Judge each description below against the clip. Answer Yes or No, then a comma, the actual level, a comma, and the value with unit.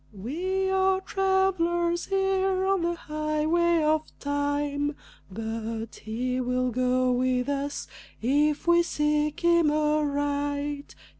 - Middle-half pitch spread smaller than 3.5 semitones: No, average, 4.1 semitones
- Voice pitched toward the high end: Yes, very high, 300 Hz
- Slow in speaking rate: Yes, slow, 105 wpm